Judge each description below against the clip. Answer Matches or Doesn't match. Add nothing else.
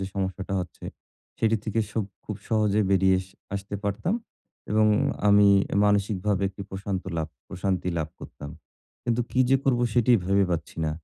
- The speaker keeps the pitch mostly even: Matches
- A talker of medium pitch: Doesn't match